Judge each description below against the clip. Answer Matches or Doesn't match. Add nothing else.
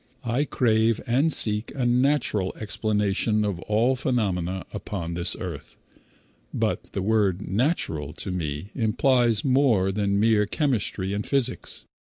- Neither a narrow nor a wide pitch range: Matches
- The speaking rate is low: Matches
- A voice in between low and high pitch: Doesn't match